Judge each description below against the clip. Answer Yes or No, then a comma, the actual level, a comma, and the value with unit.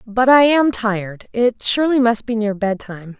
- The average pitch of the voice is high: Yes, high, 230 Hz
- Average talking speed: Yes, average, 190 wpm